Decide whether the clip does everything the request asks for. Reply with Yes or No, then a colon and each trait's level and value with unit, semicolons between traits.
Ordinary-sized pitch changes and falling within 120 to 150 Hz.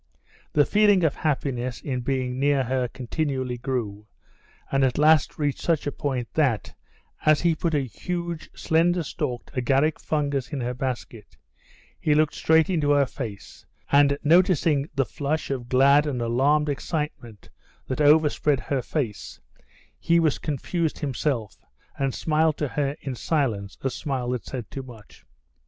Yes: average, 3.4 semitones; medium, 140 Hz